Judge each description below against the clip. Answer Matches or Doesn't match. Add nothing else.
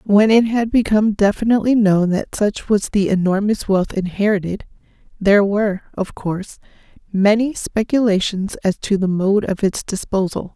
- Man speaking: Doesn't match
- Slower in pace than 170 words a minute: Matches